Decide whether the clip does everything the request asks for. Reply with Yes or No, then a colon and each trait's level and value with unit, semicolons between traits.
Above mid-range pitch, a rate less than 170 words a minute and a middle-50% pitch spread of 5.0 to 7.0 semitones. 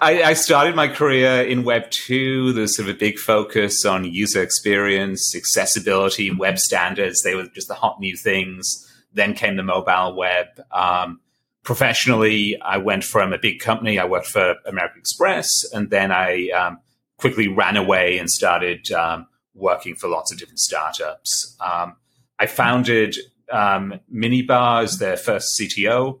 No: low, 105 Hz; average, 160 wpm; wide, 5.4 semitones